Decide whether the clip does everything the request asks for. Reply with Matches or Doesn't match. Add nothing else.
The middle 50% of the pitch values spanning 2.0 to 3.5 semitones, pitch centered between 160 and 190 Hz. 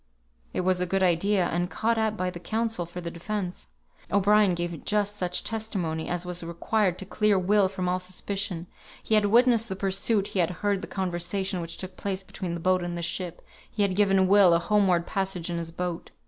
Matches